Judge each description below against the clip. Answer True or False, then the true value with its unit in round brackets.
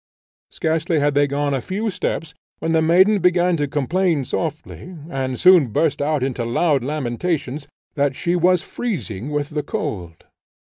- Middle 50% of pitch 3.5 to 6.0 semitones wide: True (4.1 semitones)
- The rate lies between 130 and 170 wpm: True (155 wpm)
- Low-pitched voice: False (150 Hz)